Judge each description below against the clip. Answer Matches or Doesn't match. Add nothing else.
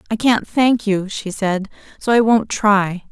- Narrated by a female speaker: Matches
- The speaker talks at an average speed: Matches